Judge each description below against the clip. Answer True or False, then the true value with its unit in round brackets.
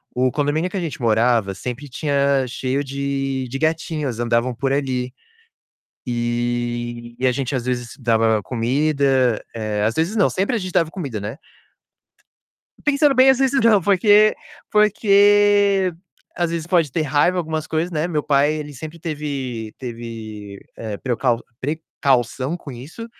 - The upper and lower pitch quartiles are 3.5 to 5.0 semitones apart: False (5.6 semitones)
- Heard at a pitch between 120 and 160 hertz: True (140 Hz)